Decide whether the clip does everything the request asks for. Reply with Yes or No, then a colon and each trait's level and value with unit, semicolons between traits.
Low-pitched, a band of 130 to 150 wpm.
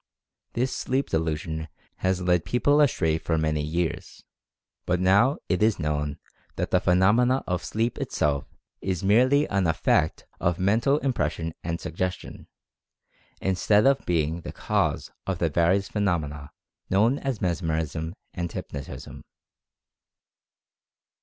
Yes: very low, 90 Hz; slow, 135 wpm